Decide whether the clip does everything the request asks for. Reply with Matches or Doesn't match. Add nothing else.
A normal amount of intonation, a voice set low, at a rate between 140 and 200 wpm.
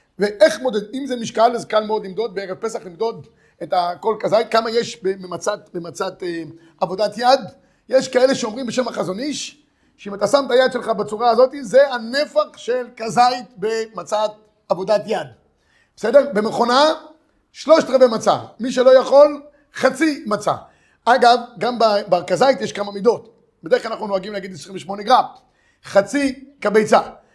Doesn't match